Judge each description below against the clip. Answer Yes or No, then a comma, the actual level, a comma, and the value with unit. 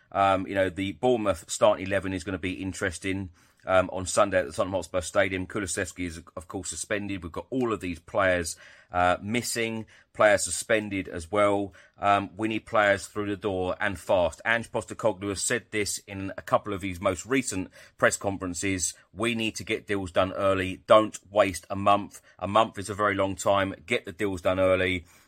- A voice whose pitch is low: Yes, low, 100 Hz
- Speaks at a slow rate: No, average, 195 wpm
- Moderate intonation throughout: No, narrow, 2.2 semitones